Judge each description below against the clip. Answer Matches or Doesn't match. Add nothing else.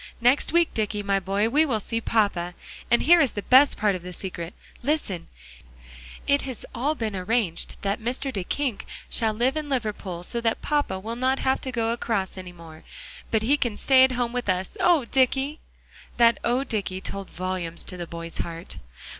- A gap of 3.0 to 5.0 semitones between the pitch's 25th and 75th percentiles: Doesn't match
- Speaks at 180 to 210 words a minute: Matches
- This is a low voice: Doesn't match